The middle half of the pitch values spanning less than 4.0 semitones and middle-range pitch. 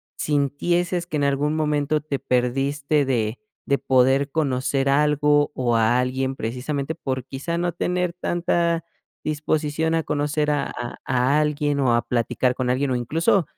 Yes: average, 2.9 semitones; medium, 145 Hz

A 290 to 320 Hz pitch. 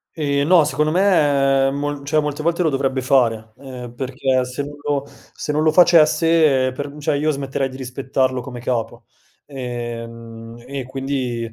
No: low, 135 Hz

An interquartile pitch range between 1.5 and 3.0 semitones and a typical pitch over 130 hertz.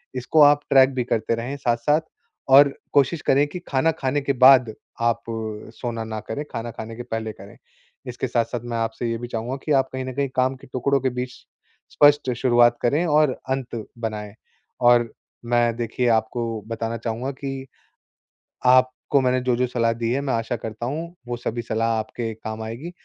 No: narrow, 2.6 semitones; low, 125 Hz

